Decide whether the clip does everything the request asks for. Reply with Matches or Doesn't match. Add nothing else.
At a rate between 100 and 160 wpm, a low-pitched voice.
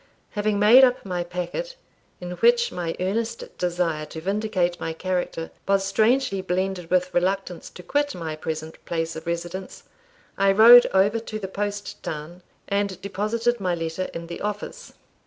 Doesn't match